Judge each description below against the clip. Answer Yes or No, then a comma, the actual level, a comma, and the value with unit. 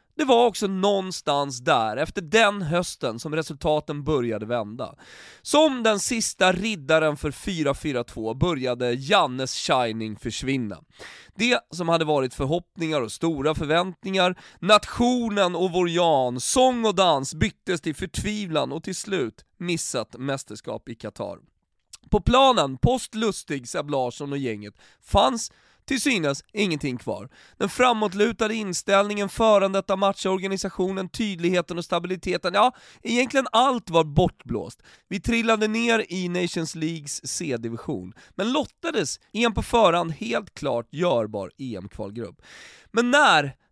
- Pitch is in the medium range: Yes, medium, 175 Hz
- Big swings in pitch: Yes, wide, 6.7 semitones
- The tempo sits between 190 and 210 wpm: No, slow, 125 wpm